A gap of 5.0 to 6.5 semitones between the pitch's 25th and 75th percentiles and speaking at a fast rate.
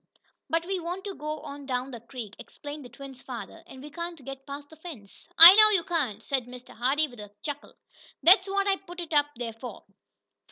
Yes: average, 5.3 semitones; fast, 215 wpm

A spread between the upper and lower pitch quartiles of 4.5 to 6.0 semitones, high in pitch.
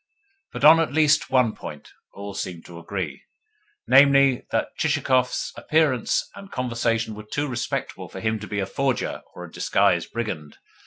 No: average, 4.9 semitones; low, 120 Hz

